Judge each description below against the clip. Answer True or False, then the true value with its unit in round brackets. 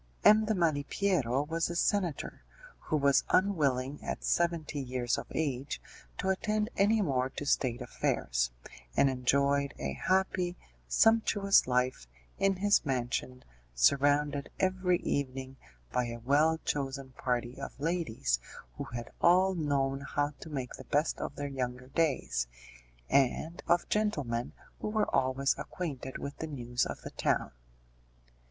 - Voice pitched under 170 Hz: True (140 Hz)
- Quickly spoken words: False (140 wpm)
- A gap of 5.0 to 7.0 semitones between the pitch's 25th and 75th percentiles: True (5.3 semitones)